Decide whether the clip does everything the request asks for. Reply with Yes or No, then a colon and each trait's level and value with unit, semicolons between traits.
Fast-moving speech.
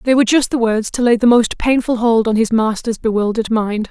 Yes: fast, 245 wpm